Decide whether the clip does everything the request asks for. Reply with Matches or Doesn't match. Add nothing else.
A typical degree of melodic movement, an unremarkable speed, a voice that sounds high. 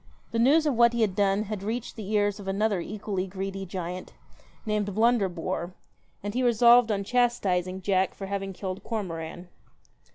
Matches